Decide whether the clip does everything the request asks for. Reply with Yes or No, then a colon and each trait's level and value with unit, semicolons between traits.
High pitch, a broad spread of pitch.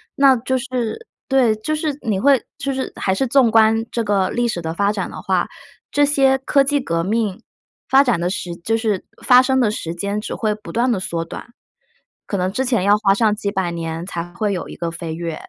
Yes: high, 220 Hz; wide, 5.7 semitones